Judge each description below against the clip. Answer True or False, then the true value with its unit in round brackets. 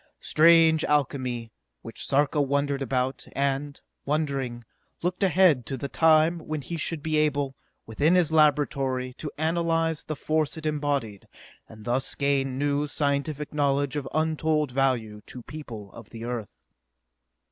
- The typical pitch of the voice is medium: True (145 Hz)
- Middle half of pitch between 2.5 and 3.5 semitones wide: True (2.8 semitones)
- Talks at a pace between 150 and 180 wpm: False (140 wpm)